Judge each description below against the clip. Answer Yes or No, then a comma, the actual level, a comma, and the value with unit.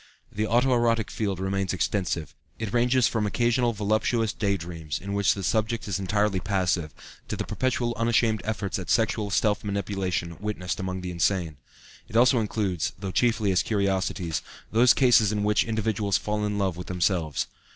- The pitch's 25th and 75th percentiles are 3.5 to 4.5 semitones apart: No, average, 3.1 semitones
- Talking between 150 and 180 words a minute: Yes, average, 170 wpm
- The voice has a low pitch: Yes, low, 100 Hz